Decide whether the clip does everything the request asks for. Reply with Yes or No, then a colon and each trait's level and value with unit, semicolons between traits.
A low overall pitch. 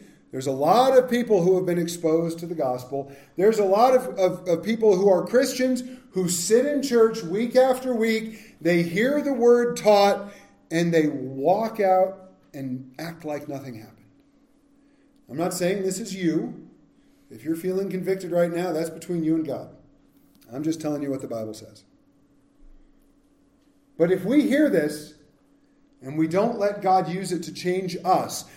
No: medium, 185 Hz